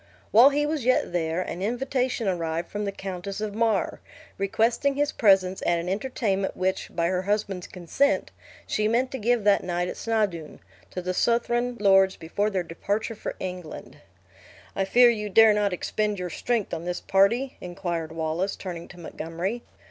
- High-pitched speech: Yes, high, 195 Hz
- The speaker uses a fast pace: No, average, 170 wpm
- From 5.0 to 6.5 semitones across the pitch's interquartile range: No, average, 4.2 semitones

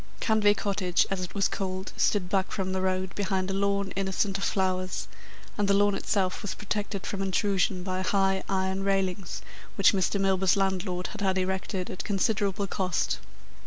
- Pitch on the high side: Yes, high, 195 Hz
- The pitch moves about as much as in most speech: No, narrow, 1.2 semitones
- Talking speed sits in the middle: Yes, average, 170 wpm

